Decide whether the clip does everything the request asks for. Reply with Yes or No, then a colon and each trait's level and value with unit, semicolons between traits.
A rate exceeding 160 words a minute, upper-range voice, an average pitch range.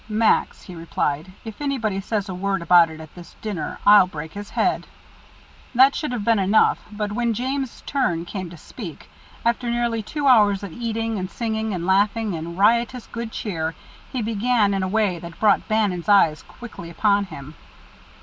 Yes: average, 180 wpm; high, 205 Hz; average, 4.2 semitones